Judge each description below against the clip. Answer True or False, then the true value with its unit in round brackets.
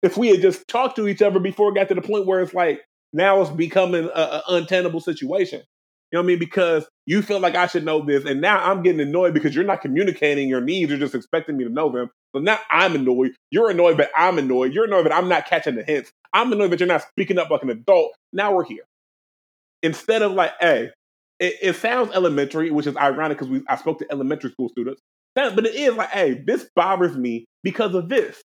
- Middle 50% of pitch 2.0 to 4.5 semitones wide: False (5.4 semitones)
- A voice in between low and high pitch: True (180 Hz)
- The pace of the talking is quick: True (240 wpm)